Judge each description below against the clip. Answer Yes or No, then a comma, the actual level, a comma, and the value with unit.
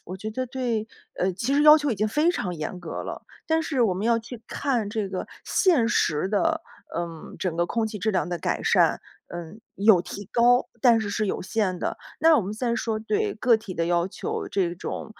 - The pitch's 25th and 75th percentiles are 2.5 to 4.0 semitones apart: No, average, 5.1 semitones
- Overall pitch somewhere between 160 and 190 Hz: No, high, 215 Hz